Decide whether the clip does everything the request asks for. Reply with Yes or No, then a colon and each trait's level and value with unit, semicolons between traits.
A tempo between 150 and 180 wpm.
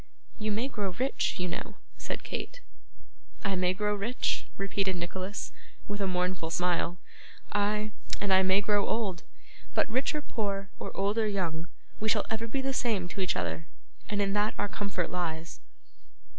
Yes: average, 170 wpm